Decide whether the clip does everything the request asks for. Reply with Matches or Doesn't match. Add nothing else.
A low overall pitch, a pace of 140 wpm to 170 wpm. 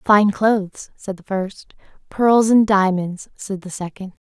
Doesn't match